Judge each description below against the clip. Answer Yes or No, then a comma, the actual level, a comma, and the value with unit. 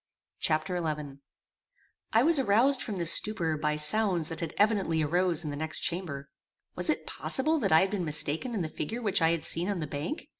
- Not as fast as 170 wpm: No, average, 200 wpm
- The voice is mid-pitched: Yes, medium, 170 Hz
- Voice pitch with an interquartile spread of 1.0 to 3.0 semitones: No, average, 5.2 semitones